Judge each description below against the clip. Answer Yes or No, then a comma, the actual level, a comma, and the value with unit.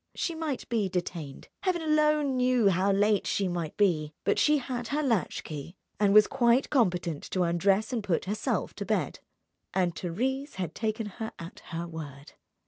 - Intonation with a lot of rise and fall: Yes, wide, 6.6 semitones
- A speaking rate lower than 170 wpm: No, average, 175 wpm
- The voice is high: Yes, high, 205 Hz